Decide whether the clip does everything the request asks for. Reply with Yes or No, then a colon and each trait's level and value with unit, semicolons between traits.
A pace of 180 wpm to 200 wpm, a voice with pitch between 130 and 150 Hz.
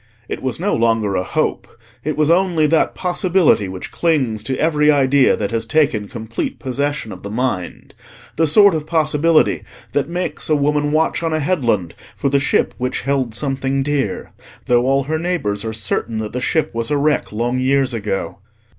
Yes: average, 185 wpm; low, 135 Hz